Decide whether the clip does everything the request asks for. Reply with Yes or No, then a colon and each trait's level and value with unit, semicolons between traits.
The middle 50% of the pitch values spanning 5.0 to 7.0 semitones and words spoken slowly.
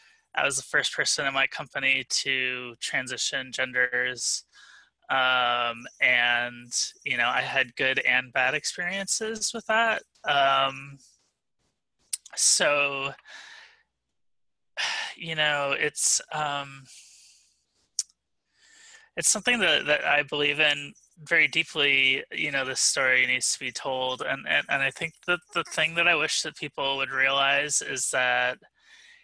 Yes: average, 5.3 semitones; slow, 130 wpm